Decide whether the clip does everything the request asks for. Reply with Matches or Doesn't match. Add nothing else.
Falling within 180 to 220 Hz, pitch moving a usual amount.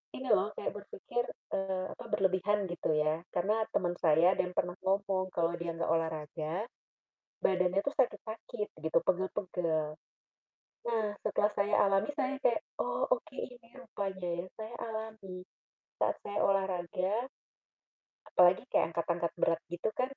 Matches